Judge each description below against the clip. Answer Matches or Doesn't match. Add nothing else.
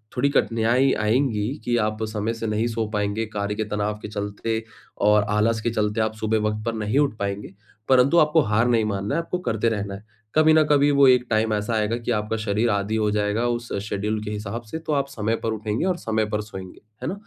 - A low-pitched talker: Matches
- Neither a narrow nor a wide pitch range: Doesn't match